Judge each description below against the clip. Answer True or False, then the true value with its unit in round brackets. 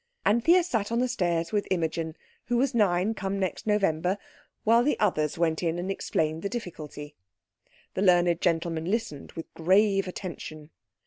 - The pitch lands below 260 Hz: True (185 Hz)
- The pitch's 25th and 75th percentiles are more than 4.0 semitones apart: True (4.5 semitones)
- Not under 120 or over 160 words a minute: True (155 wpm)